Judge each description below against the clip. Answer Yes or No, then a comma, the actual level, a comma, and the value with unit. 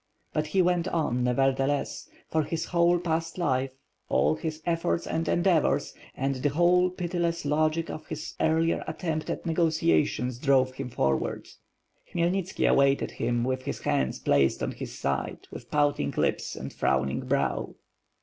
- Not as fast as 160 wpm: Yes, average, 150 wpm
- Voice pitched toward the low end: No, medium, 155 Hz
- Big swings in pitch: No, average, 4.5 semitones